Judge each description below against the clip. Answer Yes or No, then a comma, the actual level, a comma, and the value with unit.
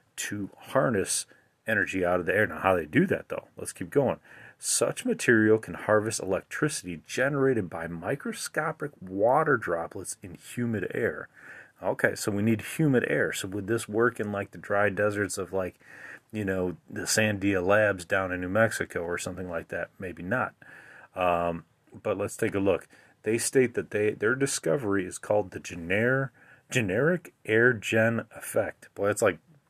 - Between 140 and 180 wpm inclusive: Yes, average, 170 wpm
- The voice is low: Yes, low, 105 Hz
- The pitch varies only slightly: No, average, 3.7 semitones